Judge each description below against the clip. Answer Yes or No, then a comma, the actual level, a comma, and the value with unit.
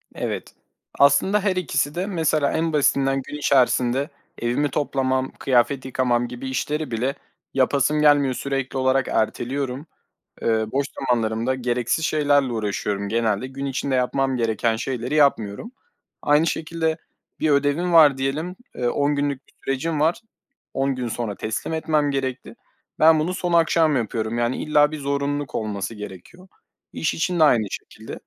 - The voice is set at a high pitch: No, low, 135 Hz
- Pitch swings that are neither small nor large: Yes, average, 3.7 semitones